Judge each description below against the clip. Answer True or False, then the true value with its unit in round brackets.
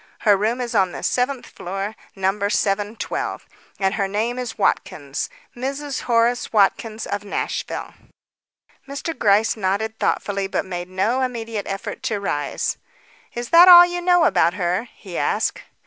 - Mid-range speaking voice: False (215 Hz)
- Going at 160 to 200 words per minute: False (145 wpm)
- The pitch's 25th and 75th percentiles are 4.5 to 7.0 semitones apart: False (4.1 semitones)